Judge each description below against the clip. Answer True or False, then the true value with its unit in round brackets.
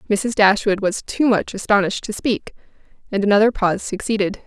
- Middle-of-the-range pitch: False (205 Hz)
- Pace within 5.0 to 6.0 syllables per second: True (5.7 syllables/s)